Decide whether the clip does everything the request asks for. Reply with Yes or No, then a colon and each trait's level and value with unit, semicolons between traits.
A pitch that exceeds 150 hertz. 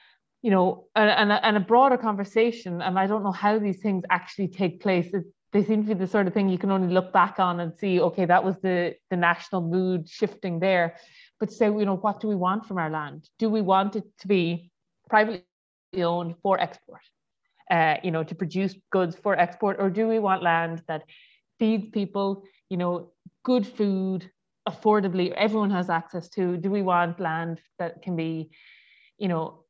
Yes: high, 190 Hz